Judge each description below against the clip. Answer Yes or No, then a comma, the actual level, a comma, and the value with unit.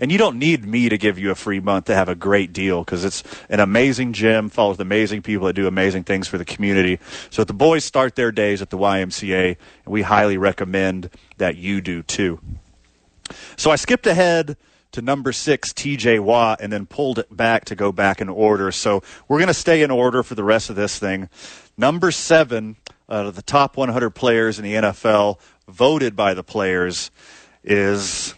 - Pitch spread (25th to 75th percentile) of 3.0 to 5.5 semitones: Yes, average, 3.7 semitones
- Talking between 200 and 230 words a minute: Yes, fast, 205 wpm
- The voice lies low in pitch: Yes, low, 105 Hz